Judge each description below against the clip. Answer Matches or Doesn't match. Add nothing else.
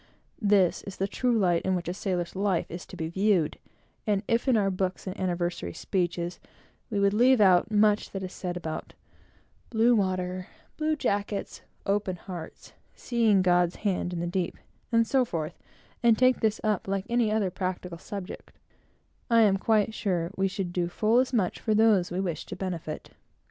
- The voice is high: Matches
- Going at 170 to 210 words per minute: Matches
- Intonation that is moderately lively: Matches